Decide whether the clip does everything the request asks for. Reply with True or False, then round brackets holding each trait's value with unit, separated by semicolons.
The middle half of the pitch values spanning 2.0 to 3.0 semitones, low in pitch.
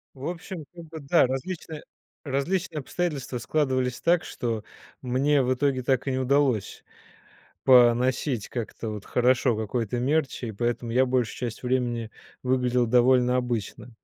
True (2.5 semitones; 130 Hz)